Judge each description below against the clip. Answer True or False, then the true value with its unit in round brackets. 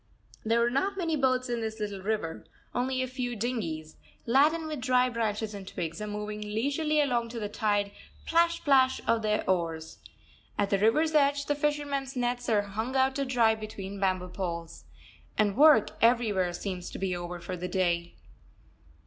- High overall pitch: True (225 Hz)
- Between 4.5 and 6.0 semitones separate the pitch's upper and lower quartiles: True (5.1 semitones)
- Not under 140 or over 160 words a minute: False (175 wpm)